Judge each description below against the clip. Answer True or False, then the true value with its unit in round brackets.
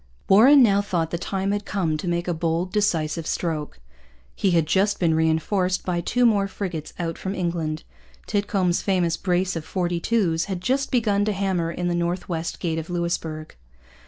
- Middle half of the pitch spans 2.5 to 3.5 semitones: True (3.2 semitones)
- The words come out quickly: False (185 wpm)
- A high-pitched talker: False (175 Hz)